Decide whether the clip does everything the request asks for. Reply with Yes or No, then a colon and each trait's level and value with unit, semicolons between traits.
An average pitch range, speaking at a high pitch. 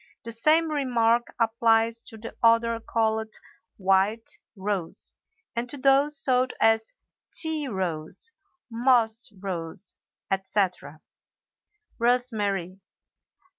Yes: average, 3.7 semitones; high, 225 Hz